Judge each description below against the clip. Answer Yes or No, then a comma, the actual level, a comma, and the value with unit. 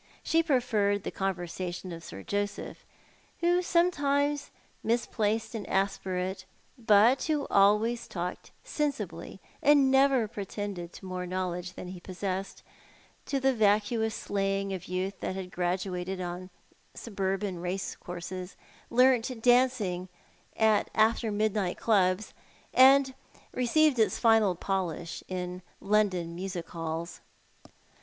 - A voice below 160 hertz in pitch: No, high, 200 Hz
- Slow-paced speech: Yes, slow, 115 wpm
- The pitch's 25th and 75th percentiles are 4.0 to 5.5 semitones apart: Yes, average, 4.4 semitones